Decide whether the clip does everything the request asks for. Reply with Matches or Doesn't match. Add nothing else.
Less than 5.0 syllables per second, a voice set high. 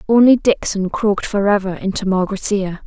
Doesn't match